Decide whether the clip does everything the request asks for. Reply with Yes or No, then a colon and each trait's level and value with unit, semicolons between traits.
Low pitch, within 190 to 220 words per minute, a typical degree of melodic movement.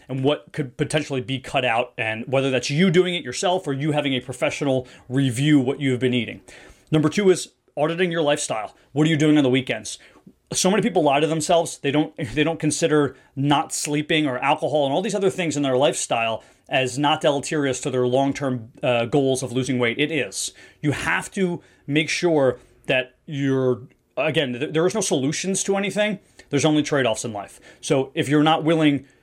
No: medium, 145 Hz; average, 200 wpm; average, 3.4 semitones